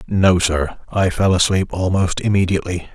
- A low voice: Yes, very low, 90 Hz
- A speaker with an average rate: Yes, average, 145 wpm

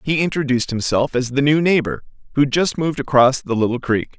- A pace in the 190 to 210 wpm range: Yes, average, 200 wpm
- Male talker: Yes, male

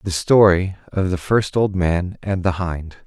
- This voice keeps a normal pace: Yes, average, 195 wpm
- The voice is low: Yes, very low, 95 Hz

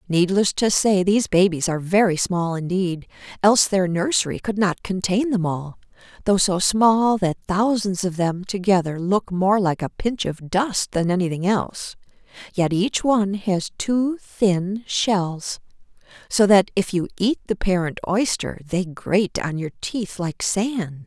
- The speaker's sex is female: Yes, female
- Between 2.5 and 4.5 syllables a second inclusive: Yes, 4.3 syllables/s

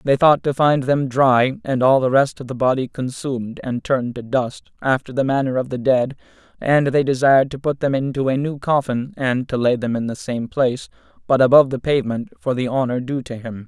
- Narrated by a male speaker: Yes, male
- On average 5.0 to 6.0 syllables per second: Yes, 5.5 syllables/s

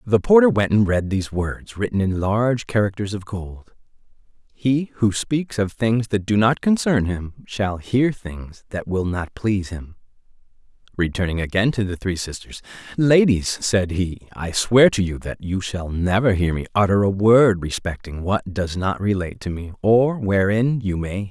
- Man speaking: Yes, male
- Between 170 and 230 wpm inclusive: Yes, average, 190 wpm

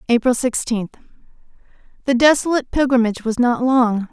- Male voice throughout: No, female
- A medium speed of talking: No, slow, 100 wpm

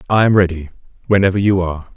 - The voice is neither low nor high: No, very low, 95 Hz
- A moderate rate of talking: Yes, average, 185 wpm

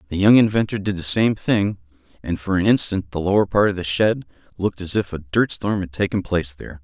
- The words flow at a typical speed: No, fast, 230 wpm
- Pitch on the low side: Yes, very low, 95 Hz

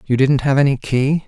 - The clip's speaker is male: Yes, male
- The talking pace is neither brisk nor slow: No, fast, 235 wpm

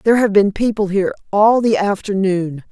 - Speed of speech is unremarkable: Yes, average, 175 wpm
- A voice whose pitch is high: Yes, high, 200 Hz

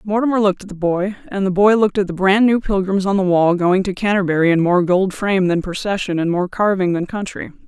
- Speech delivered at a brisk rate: Yes, fast, 240 wpm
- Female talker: Yes, female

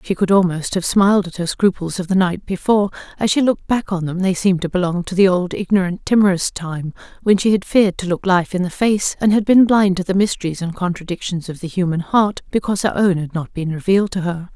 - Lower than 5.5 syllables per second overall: No, 6.1 syllables/s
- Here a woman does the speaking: Yes, female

